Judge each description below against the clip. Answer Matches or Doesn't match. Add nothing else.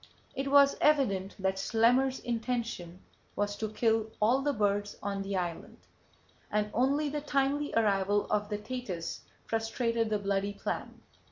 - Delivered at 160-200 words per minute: Doesn't match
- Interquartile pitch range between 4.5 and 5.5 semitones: Doesn't match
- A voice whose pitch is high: Matches